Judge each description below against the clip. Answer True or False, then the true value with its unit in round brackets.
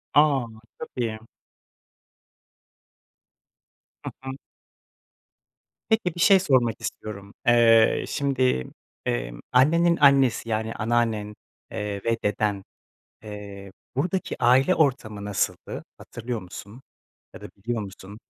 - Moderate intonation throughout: True (4.6 semitones)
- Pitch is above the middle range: False (115 Hz)